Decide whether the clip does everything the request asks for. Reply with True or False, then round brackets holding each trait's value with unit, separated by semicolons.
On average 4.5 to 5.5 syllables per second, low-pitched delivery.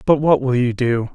True (5.0 syllables/s; 130 Hz)